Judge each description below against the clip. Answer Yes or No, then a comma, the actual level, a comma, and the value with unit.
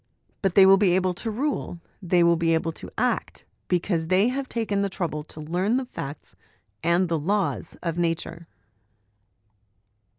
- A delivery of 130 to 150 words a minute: No, average, 165 wpm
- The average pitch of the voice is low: No, medium, 180 Hz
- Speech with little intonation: No, average, 3.2 semitones